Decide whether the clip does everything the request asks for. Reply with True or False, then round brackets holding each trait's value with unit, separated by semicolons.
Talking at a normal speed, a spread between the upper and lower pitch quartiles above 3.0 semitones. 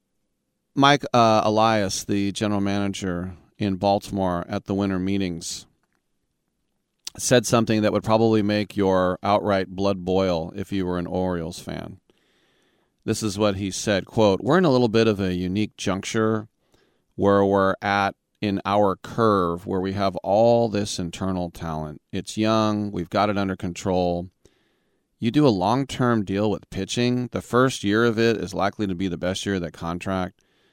False (165 wpm; 2.7 semitones)